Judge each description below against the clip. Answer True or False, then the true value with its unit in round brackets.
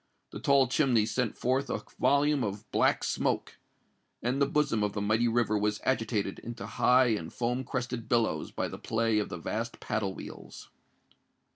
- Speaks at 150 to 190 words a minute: True (170 wpm)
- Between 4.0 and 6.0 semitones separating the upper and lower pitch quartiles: False (3.2 semitones)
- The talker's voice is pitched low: True (115 Hz)